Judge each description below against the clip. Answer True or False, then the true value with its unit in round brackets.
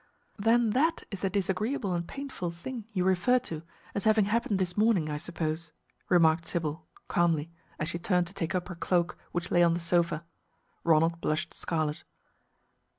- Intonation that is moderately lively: True (3.4 semitones)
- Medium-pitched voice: True (175 Hz)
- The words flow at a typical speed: True (170 wpm)